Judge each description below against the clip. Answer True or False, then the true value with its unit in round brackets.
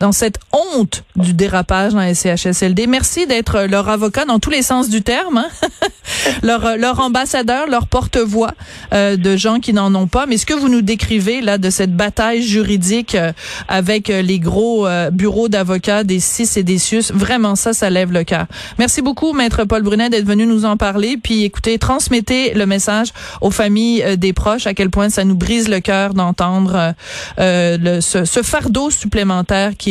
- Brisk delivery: False (195 wpm)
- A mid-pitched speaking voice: False (210 Hz)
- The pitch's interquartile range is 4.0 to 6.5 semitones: False (3.2 semitones)